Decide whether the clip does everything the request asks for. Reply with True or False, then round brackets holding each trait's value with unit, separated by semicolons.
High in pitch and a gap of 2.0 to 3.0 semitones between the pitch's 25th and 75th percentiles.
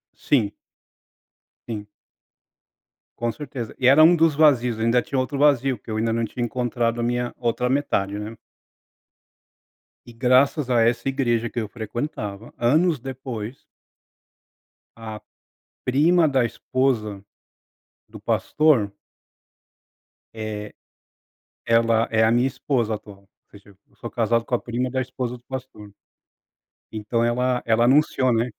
False (120 Hz; 2.7 semitones)